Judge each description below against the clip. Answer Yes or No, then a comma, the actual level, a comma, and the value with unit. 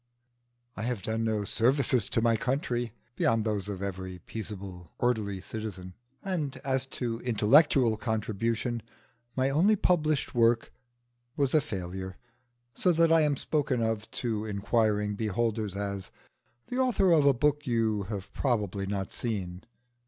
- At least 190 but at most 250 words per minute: No, average, 140 wpm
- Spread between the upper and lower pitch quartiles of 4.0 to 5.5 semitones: Yes, average, 4.6 semitones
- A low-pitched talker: Yes, low, 115 Hz